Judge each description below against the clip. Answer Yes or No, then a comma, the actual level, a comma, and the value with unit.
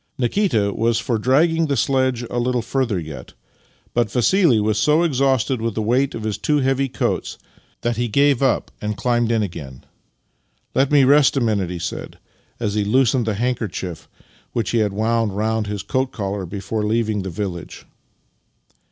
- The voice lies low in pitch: Yes, low, 115 Hz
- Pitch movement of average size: Yes, average, 3.9 semitones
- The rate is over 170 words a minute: Yes, average, 180 wpm